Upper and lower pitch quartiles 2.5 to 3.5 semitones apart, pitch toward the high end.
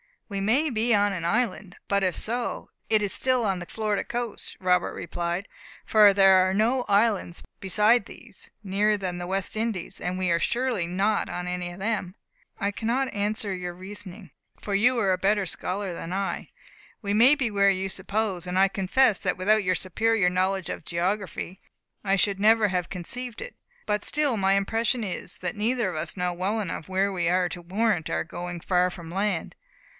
Yes: average, 3.0 semitones; high, 195 Hz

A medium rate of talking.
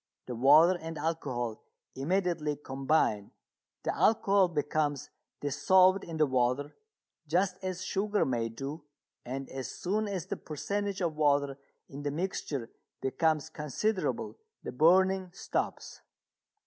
No: slow, 120 wpm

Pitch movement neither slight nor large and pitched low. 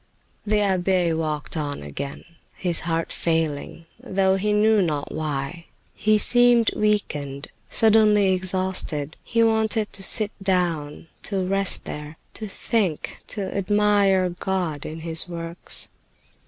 No: average, 4.4 semitones; medium, 185 Hz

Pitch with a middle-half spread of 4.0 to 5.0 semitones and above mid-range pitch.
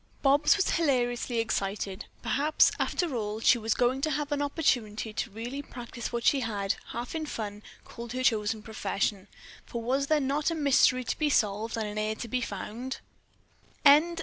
Yes: average, 4.4 semitones; high, 240 Hz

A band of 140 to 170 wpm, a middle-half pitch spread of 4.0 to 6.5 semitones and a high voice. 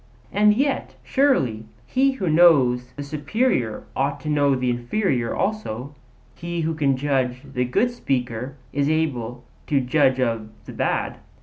No: average, 150 wpm; average, 5.3 semitones; medium, 140 Hz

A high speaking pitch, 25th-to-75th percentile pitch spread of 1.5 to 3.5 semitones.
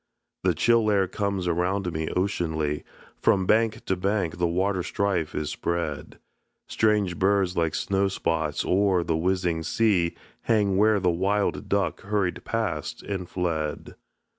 No: very low, 95 Hz; average, 3.0 semitones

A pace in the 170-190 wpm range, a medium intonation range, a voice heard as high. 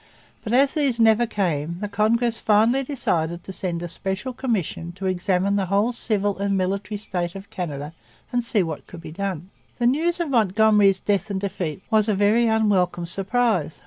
Yes: average, 180 wpm; average, 3.8 semitones; high, 200 Hz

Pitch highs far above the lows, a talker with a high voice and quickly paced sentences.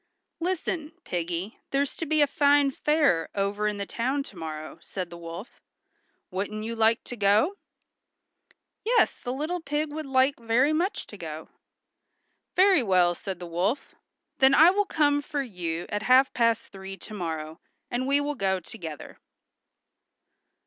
No: wide, 7.4 semitones; high, 230 Hz; average, 155 wpm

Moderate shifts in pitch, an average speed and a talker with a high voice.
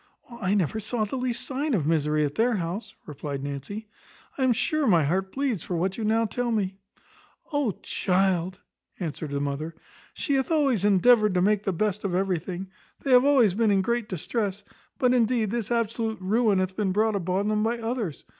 Yes: average, 4.4 semitones; average, 190 wpm; high, 205 Hz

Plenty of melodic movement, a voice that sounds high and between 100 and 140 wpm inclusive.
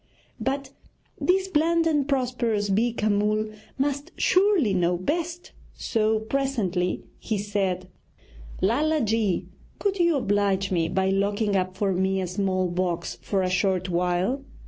Yes: wide, 6.5 semitones; high, 205 Hz; slow, 135 wpm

